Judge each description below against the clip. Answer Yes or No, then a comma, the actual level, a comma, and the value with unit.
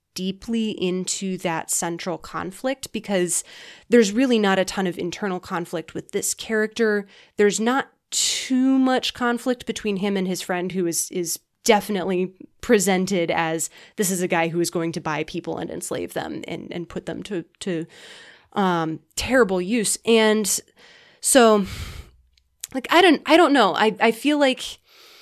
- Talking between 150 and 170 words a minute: Yes, average, 160 wpm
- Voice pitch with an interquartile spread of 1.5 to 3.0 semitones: No, average, 5.0 semitones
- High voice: Yes, high, 195 Hz